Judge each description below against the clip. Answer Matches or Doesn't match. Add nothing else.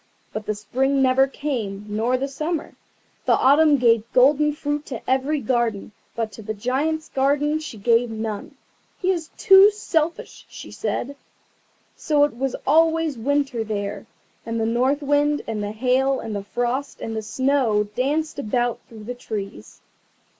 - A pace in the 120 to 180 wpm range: Matches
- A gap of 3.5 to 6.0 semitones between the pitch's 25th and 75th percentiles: Matches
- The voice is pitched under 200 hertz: Doesn't match